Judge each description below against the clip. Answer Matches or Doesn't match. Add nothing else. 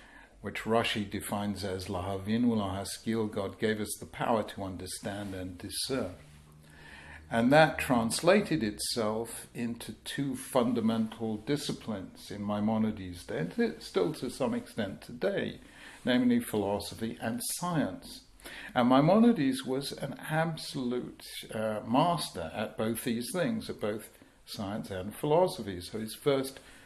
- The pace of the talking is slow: Doesn't match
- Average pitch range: Matches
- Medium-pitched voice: Doesn't match